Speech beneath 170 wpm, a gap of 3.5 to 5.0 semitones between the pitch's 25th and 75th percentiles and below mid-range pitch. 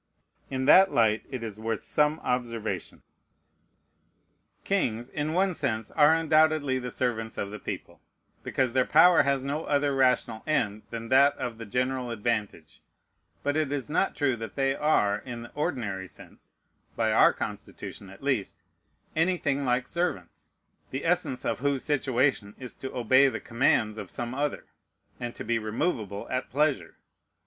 Yes: average, 155 wpm; average, 4.4 semitones; low, 130 Hz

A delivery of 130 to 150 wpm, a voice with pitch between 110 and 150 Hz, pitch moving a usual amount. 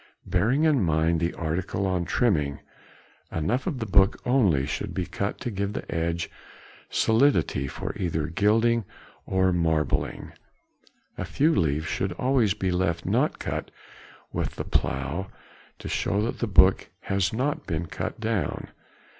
No: average, 145 wpm; very low, 95 Hz; average, 5.0 semitones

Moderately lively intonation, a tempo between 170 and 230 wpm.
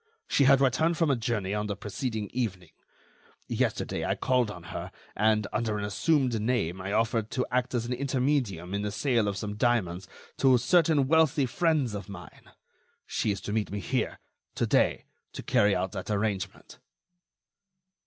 Yes: average, 4.2 semitones; average, 175 wpm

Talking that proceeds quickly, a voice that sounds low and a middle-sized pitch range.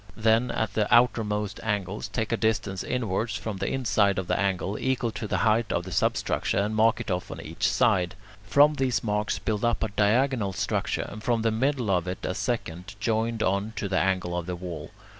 Yes: fast, 210 wpm; low, 105 Hz; average, 3.1 semitones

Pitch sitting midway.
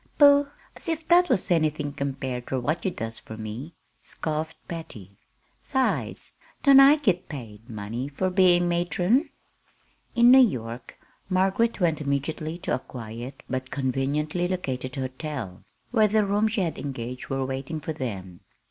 Yes: medium, 150 Hz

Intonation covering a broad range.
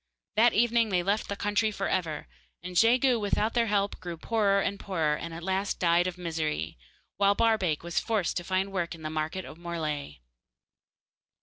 No: average, 3.7 semitones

